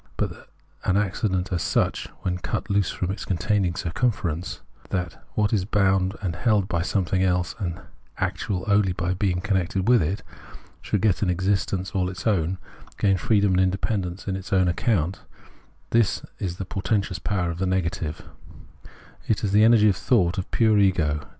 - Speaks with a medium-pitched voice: No, very low, 95 Hz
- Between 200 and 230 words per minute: No, average, 180 wpm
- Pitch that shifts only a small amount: Yes, narrow, 2.3 semitones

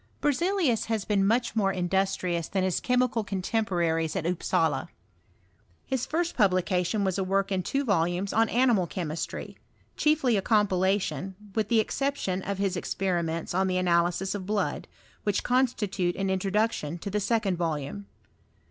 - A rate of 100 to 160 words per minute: Yes, average, 155 wpm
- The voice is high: Yes, high, 195 Hz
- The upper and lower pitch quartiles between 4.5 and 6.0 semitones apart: No, average, 3.6 semitones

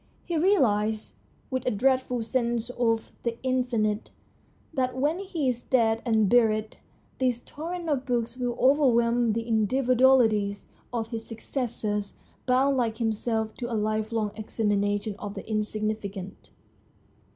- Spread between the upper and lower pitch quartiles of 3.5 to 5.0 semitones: No, average, 2.9 semitones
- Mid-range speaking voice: No, high, 230 Hz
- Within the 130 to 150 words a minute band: Yes, slow, 135 wpm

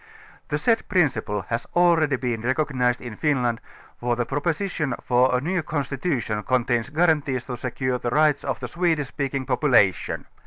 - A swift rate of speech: No, average, 160 wpm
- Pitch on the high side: No, low, 130 Hz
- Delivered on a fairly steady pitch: No, average, 4.0 semitones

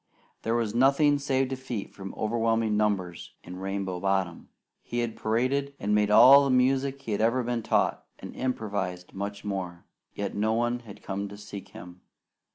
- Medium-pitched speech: No, low, 110 Hz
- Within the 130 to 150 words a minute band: No, average, 170 wpm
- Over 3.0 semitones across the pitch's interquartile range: Yes, average, 4.3 semitones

